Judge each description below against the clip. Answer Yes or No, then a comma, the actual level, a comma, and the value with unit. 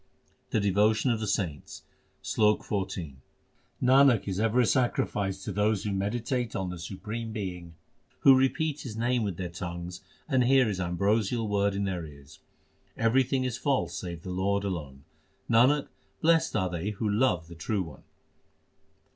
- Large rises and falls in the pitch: No, average, 4.7 semitones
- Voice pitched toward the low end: Yes, low, 105 Hz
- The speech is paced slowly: No, average, 160 wpm